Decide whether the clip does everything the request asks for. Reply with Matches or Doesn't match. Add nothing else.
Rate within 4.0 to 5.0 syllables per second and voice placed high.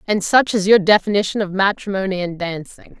Doesn't match